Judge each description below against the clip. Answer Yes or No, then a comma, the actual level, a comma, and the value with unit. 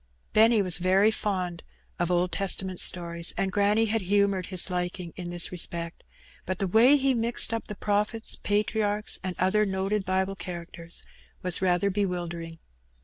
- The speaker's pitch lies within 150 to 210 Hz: Yes, high, 190 Hz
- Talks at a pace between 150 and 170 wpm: Yes, average, 155 wpm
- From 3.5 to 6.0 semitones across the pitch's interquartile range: No, average, 2.8 semitones